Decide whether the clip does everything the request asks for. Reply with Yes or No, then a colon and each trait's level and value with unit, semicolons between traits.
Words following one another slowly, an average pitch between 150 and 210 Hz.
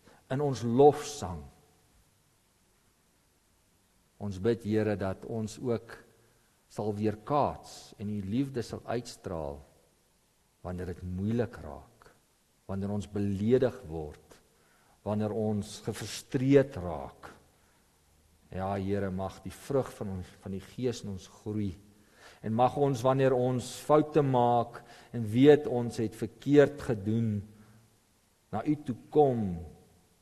No: slow, 115 wpm; low, 105 Hz